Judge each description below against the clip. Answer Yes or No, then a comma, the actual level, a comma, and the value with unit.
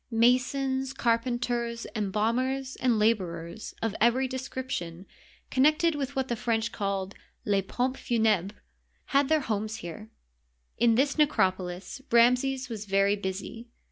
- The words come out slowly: Yes, slow, 130 wpm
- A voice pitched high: Yes, high, 235 Hz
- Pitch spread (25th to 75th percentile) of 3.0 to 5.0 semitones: Yes, average, 4.2 semitones